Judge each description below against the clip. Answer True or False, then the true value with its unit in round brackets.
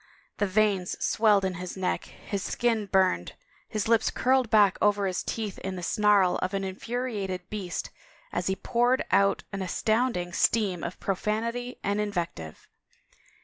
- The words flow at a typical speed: True (150 wpm)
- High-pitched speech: True (200 Hz)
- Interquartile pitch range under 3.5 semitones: True (2.9 semitones)